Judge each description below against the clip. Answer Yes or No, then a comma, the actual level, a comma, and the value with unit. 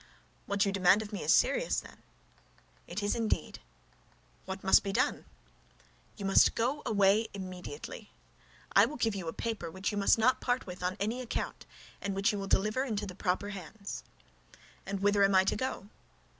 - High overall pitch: Yes, high, 200 Hz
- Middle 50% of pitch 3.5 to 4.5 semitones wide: No, narrow, 2.5 semitones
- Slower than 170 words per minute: No, average, 185 wpm